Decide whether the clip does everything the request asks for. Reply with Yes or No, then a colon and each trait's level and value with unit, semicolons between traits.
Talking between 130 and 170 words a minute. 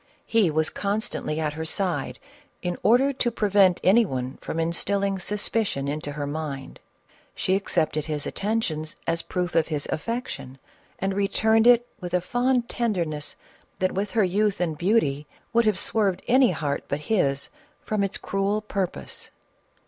Yes: average, 155 wpm